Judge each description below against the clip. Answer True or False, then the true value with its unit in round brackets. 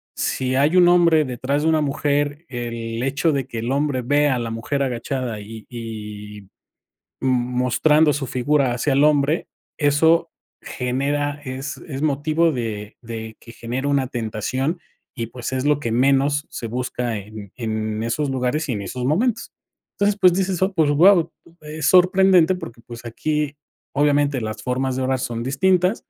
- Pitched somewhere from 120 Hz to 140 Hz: True (135 Hz)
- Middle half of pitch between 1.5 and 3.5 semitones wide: False (4.1 semitones)